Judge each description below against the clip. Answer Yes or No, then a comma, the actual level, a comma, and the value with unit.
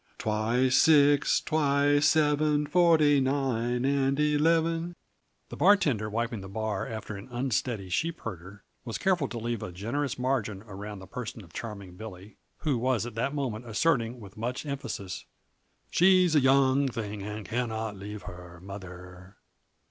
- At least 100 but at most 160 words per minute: Yes, average, 150 wpm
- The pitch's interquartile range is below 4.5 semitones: No, wide, 5.5 semitones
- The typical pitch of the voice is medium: No, low, 120 Hz